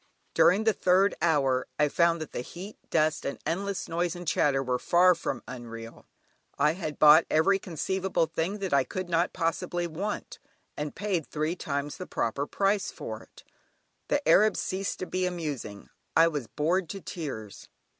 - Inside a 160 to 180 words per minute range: Yes, average, 170 wpm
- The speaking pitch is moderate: Yes, medium, 165 Hz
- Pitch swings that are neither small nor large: Yes, average, 4.0 semitones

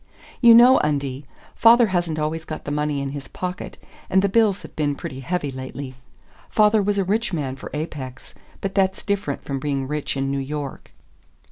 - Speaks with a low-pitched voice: No, medium, 150 Hz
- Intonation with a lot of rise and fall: Yes, wide, 6.0 semitones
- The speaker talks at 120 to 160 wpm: No, average, 190 wpm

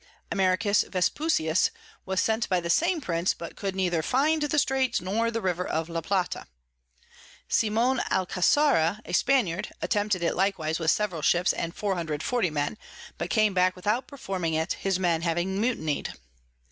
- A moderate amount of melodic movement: Yes, average, 4.8 semitones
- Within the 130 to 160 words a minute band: Yes, average, 155 wpm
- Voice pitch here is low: No, high, 190 Hz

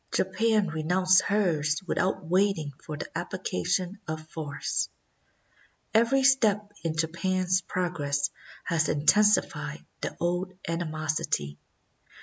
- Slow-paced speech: Yes, slow, 100 wpm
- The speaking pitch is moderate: Yes, medium, 175 Hz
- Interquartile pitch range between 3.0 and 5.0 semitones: Yes, average, 3.9 semitones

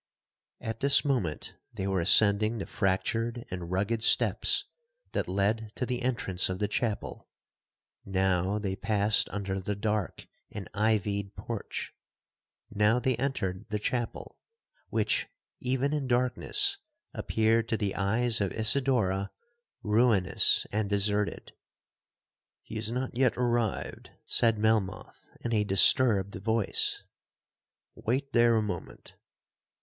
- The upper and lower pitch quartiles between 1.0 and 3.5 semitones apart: Yes, average, 3.2 semitones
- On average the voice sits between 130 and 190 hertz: No, low, 110 Hz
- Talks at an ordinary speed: No, slow, 120 wpm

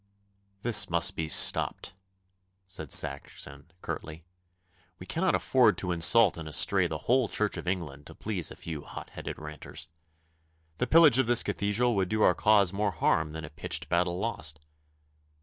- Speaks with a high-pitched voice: No, very low, 90 Hz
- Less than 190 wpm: Yes, average, 165 wpm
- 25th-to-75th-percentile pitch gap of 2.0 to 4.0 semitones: No, wide, 5.5 semitones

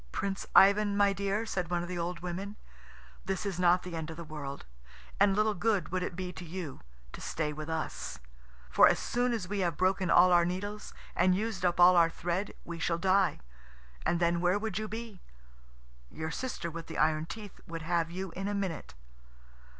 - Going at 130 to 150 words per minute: No, fast, 205 wpm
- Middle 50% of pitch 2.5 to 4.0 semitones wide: Yes, average, 2.8 semitones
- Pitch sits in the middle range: Yes, medium, 180 Hz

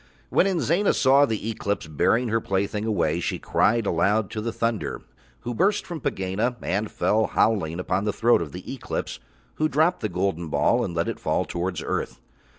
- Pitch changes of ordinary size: Yes, average, 4.6 semitones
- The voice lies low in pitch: Yes, low, 110 Hz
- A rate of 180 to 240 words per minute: Yes, average, 185 wpm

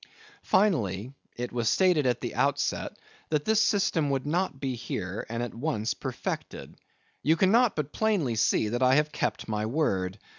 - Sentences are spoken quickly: No, average, 170 wpm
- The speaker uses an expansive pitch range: Yes, wide, 5.7 semitones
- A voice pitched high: No, low, 135 Hz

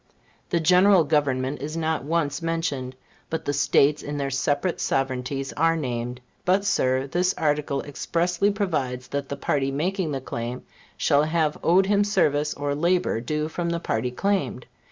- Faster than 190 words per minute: No, average, 160 wpm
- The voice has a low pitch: No, medium, 150 Hz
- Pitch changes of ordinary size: Yes, average, 3.9 semitones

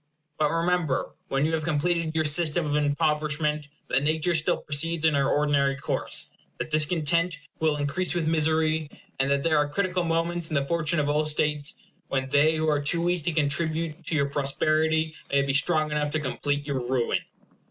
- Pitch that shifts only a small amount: Yes, narrow, 2.2 semitones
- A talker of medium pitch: Yes, medium, 155 Hz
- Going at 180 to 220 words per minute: Yes, average, 185 wpm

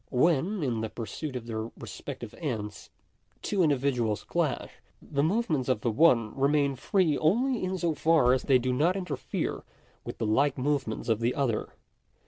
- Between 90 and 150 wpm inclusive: No, average, 165 wpm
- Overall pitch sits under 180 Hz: Yes, medium, 140 Hz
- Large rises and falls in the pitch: Yes, wide, 5.7 semitones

